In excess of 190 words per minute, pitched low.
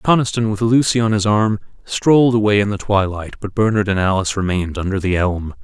Yes: average, 200 wpm; low, 105 Hz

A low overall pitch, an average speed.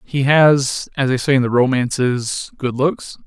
Yes: low, 130 Hz; average, 145 wpm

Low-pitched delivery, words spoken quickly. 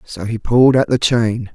Yes: low, 115 Hz; fast, 235 wpm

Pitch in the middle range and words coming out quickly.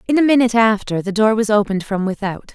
No: high, 215 Hz; fast, 235 wpm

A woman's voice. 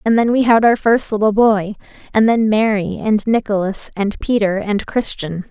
Yes: female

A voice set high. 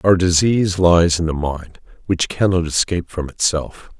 No: very low, 85 Hz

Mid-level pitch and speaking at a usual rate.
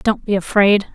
No: high, 200 Hz; average, 190 wpm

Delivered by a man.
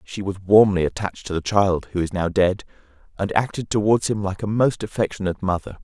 Yes: male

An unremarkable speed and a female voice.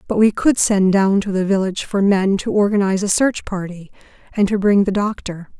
No: fast, 215 wpm; female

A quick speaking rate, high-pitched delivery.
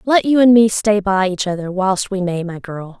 Yes: fast, 260 wpm; high, 200 Hz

